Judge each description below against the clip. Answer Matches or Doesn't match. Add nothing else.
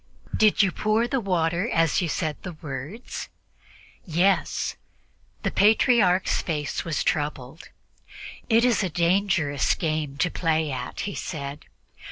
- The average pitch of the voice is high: Doesn't match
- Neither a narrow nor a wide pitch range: Matches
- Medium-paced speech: Doesn't match